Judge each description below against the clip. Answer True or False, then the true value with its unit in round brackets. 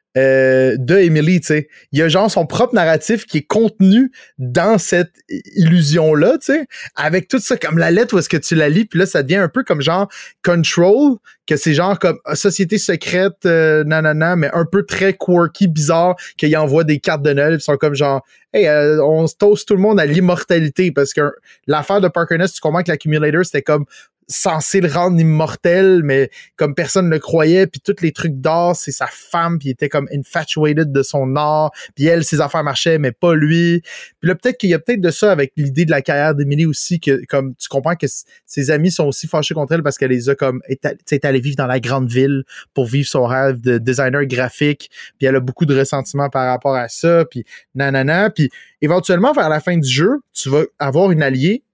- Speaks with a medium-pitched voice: True (160 Hz)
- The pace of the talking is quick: True (225 wpm)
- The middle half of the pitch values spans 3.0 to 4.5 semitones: True (4.1 semitones)